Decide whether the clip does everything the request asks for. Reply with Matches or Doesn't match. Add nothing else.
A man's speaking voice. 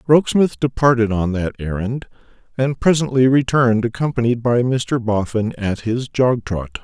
Matches